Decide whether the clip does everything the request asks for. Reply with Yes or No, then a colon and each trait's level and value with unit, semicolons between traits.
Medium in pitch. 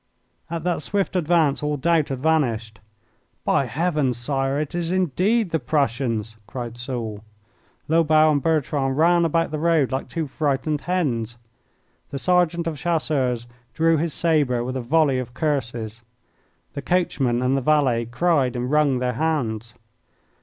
Yes: medium, 145 Hz